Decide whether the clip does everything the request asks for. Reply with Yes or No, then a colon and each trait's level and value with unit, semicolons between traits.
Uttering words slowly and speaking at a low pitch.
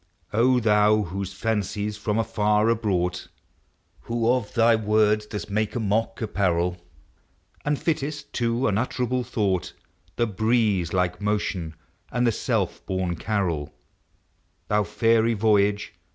Yes: slow, 125 wpm; low, 105 Hz